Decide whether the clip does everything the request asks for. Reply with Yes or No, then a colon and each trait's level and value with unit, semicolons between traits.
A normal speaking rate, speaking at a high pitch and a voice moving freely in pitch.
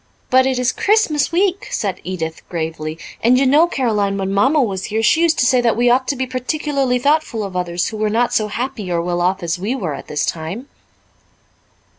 No: fast, 215 wpm; high, 230 Hz; wide, 6.2 semitones